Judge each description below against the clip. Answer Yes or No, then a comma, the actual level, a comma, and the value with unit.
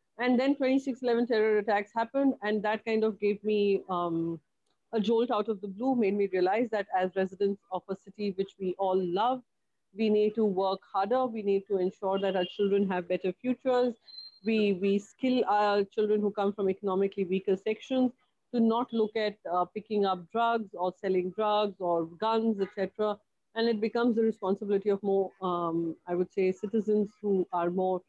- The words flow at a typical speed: Yes, average, 190 wpm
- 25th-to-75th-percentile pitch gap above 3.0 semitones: No, average, 2.7 semitones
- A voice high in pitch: Yes, high, 205 Hz